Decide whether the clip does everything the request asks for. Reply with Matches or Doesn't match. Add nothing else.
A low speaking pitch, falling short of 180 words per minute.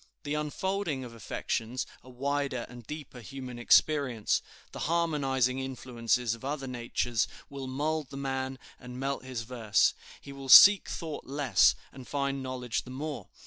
Matches